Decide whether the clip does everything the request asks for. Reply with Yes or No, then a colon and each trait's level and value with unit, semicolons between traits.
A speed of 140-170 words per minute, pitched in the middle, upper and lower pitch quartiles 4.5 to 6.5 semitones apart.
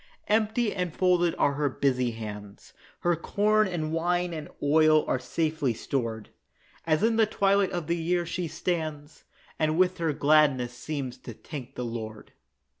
Yes: average, 160 wpm; medium, 155 Hz; average, 5.2 semitones